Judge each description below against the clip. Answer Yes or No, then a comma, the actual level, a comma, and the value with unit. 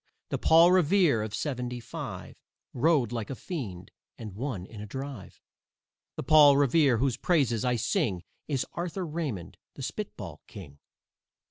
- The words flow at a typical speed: Yes, average, 145 wpm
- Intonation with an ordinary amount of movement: No, wide, 5.9 semitones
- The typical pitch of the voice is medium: No, low, 130 Hz